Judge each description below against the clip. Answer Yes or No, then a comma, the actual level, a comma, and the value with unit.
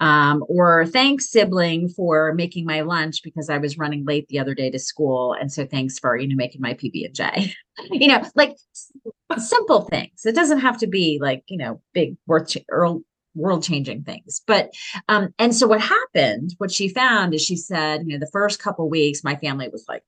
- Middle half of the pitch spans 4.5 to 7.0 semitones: Yes, wide, 5.6 semitones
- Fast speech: No, average, 195 wpm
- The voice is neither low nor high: Yes, medium, 165 Hz